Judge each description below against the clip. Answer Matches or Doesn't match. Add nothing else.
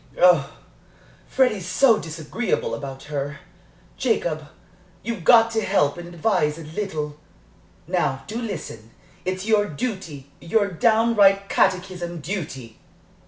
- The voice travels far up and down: Matches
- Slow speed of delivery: Matches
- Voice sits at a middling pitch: Matches